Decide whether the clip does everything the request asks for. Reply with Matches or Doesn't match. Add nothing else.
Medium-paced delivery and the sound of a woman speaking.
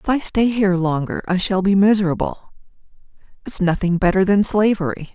Matches